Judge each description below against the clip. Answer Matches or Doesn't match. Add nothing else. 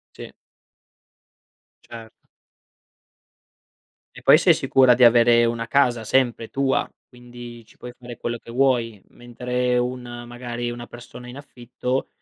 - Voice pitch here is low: Matches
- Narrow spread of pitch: Matches